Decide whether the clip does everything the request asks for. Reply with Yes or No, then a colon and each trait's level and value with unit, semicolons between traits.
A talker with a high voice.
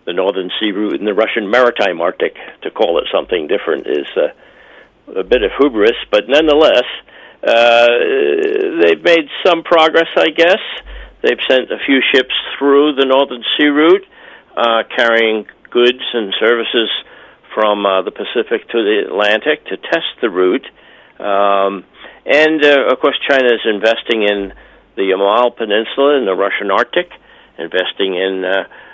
No: medium, 140 Hz